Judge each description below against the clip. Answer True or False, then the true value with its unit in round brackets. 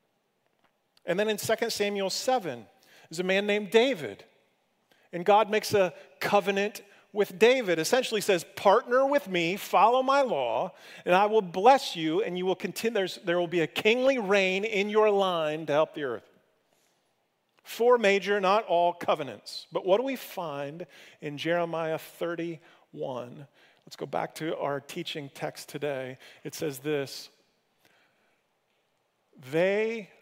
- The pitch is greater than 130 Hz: True (190 Hz)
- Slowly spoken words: False (145 wpm)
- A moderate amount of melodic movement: True (4.7 semitones)